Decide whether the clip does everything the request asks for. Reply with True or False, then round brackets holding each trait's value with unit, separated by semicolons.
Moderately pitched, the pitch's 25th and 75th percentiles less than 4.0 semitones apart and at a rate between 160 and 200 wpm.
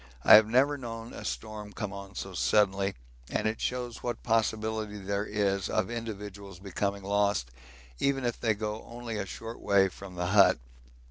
False (105 Hz; 2.4 semitones; 175 wpm)